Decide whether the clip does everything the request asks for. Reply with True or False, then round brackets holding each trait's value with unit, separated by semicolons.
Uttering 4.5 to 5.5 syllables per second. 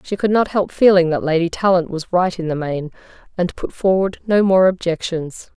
True (5.1 syllables/s)